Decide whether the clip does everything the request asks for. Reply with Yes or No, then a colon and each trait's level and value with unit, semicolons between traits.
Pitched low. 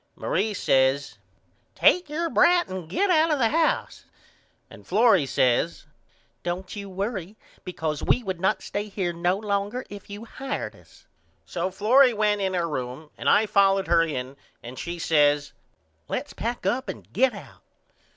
No: high, 195 Hz